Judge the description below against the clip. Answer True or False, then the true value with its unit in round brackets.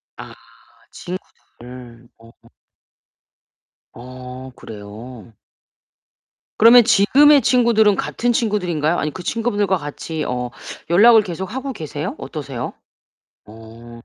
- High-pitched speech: False (160 Hz)